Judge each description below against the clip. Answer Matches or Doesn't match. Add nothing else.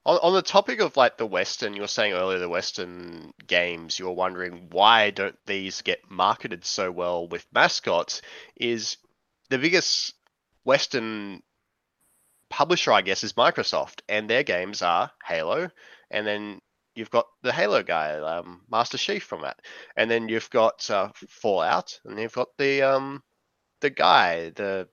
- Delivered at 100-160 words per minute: Matches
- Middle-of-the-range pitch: Doesn't match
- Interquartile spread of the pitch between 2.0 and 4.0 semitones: Doesn't match